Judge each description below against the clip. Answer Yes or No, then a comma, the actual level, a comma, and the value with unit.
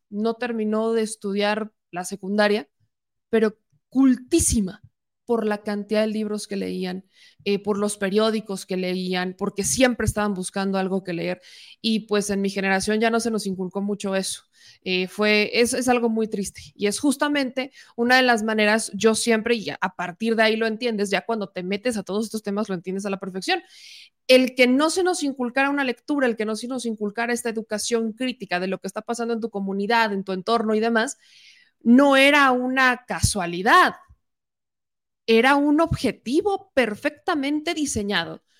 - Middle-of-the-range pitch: No, high, 220 Hz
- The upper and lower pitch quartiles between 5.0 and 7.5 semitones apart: No, average, 3.6 semitones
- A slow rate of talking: No, average, 180 wpm